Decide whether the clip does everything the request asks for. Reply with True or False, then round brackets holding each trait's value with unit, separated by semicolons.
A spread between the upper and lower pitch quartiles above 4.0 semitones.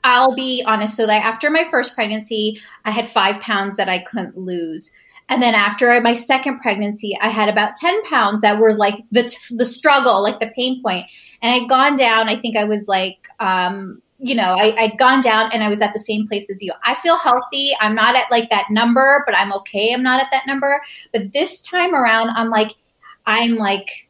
False (3.4 semitones)